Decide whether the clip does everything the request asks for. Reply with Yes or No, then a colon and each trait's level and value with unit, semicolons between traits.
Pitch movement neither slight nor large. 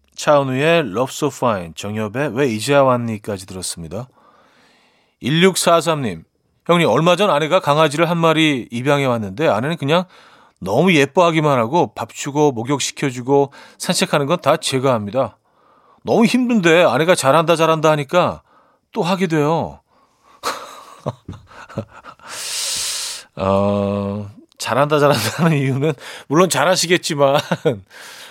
Yes: average, 5.0 semitones